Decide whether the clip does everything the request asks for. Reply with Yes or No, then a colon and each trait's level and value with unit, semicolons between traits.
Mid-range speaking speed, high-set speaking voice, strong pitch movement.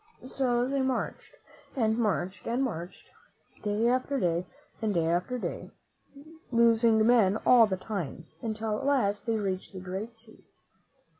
No: average, 145 wpm; high, 220 Hz; average, 4.1 semitones